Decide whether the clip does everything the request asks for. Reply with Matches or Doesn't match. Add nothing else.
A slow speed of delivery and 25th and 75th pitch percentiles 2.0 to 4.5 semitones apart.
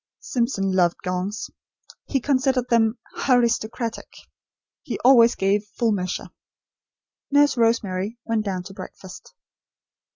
Matches